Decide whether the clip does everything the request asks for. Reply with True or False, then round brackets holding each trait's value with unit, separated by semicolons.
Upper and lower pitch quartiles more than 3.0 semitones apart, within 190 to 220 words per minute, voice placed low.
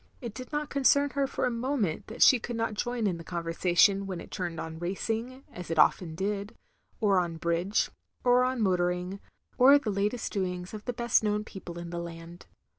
False (5.6 semitones; 200 wpm; 200 Hz)